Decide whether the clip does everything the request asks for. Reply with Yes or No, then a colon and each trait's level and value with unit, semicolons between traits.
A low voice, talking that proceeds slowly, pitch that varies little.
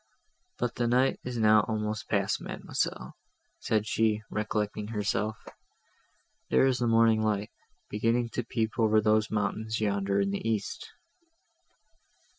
Yes: low, 110 Hz; slow, 130 wpm; narrow, 1.4 semitones